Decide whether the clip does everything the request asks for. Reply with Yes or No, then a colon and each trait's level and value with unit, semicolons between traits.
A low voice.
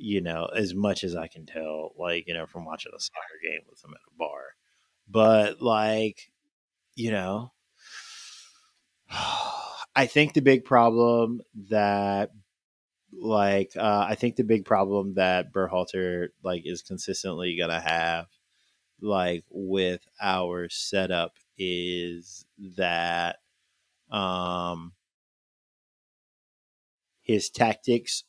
Yes: very low, 95 Hz